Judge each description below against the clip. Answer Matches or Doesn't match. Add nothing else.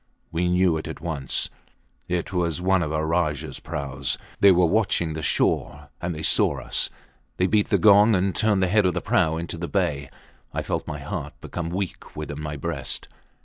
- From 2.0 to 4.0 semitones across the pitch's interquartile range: Matches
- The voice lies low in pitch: Matches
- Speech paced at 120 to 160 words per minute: Doesn't match